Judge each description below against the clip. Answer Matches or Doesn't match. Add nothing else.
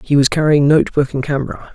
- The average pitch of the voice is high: Doesn't match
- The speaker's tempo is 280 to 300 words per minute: Doesn't match